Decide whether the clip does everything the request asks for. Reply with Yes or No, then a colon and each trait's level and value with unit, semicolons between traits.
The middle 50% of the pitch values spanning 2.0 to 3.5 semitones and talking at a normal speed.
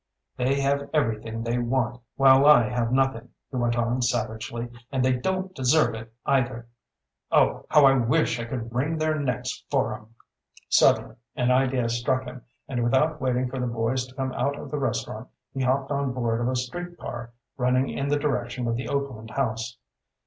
Yes: narrow, 2.5 semitones; average, 185 wpm